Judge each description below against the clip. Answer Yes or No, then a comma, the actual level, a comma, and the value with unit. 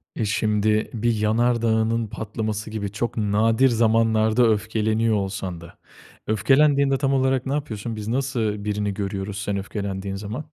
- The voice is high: No, low, 110 Hz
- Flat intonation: Yes, narrow, 2.2 semitones